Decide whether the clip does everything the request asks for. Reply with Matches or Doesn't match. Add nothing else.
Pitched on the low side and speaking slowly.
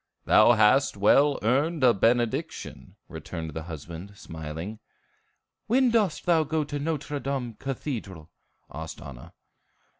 Matches